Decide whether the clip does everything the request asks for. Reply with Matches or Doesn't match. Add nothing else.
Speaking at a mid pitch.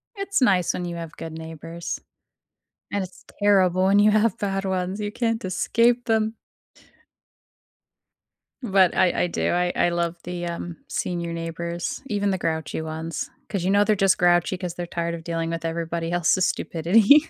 Matches